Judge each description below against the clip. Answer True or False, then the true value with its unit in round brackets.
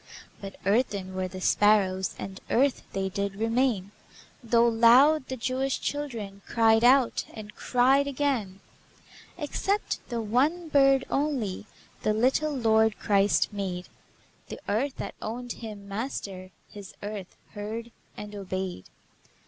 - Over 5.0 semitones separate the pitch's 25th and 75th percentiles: False (4.6 semitones)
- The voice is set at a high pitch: True (225 Hz)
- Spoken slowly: True (125 wpm)